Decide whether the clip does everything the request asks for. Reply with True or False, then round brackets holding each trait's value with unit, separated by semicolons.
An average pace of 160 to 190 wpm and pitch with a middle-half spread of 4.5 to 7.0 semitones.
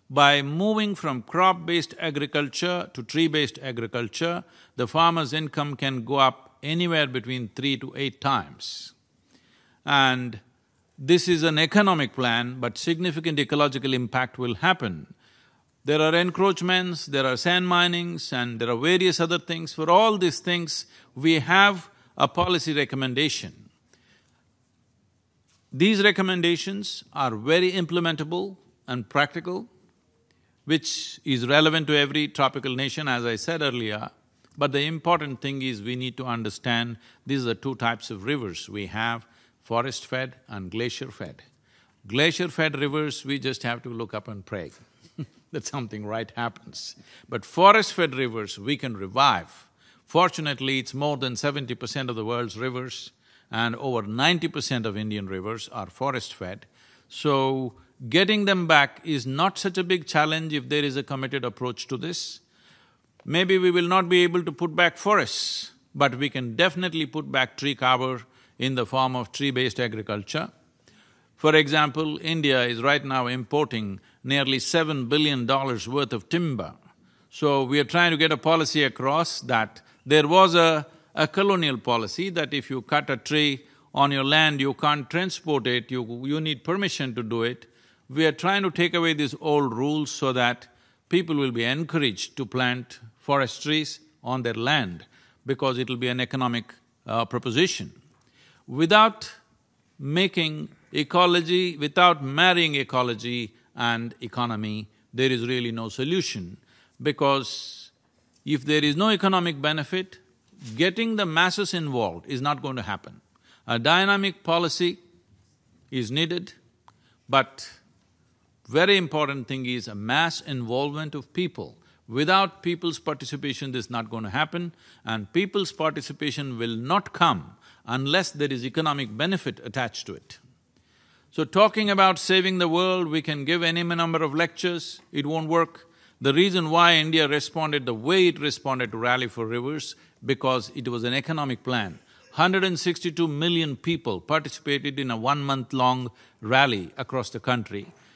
False (150 wpm; 5.0 semitones)